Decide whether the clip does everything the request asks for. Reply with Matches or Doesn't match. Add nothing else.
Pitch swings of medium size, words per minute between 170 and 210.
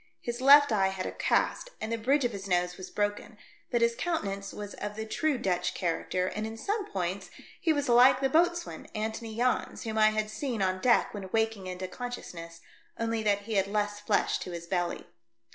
Matches